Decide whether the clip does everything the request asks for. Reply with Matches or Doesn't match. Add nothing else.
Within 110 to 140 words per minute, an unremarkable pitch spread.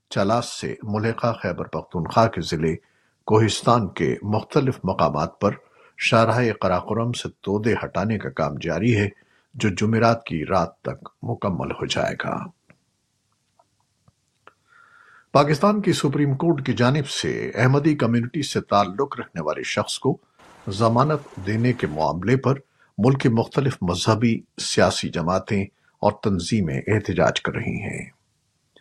Matches